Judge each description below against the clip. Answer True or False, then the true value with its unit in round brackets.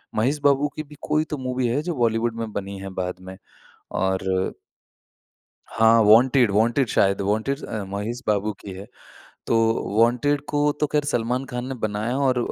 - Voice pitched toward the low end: True (115 Hz)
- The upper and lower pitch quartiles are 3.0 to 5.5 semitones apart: True (4.4 semitones)